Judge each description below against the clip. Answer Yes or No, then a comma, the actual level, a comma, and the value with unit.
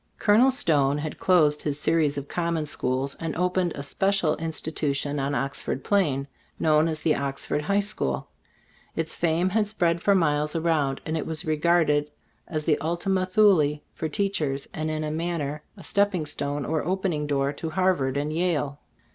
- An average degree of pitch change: Yes, average, 3.1 semitones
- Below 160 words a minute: No, average, 175 wpm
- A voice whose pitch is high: No, medium, 155 Hz